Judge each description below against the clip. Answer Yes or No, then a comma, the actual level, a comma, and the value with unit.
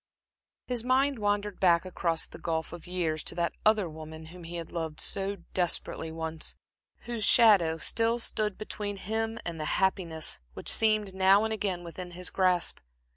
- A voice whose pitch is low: No, medium, 185 Hz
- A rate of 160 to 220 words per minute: Yes, average, 170 wpm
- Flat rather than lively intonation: No, average, 4.2 semitones